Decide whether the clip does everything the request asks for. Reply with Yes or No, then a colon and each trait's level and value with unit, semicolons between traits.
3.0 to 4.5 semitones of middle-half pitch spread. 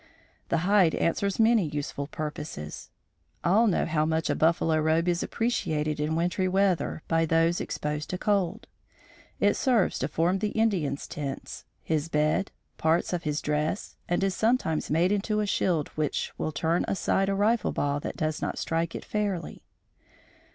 Yes: average, 4.1 semitones